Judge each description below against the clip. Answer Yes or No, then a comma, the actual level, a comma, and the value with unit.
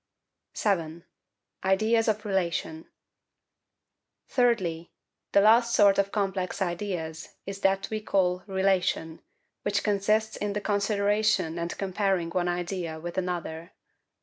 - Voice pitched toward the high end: Yes, high, 195 Hz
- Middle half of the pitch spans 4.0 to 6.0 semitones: No, average, 3.0 semitones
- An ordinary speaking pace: No, slow, 115 wpm